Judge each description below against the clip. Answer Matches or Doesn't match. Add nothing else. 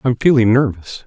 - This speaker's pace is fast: Doesn't match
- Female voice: Doesn't match